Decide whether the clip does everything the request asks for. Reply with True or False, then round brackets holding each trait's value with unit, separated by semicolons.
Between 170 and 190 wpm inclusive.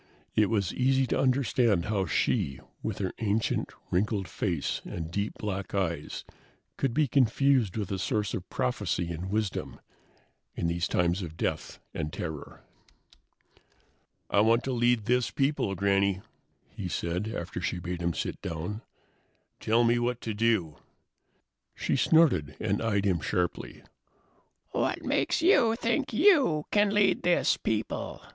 False (145 wpm)